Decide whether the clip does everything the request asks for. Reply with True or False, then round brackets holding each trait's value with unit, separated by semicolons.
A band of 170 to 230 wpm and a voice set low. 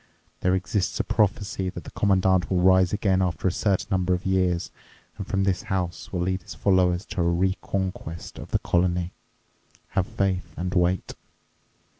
True (175 wpm; 95 Hz)